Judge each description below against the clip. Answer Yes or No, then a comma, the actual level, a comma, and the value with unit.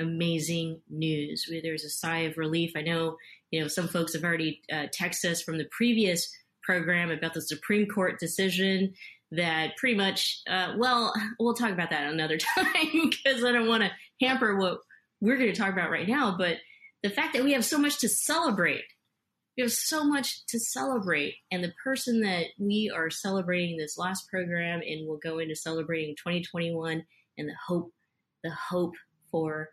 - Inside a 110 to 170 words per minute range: No, average, 185 wpm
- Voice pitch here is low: No, medium, 175 Hz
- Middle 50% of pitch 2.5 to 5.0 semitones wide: No, wide, 5.6 semitones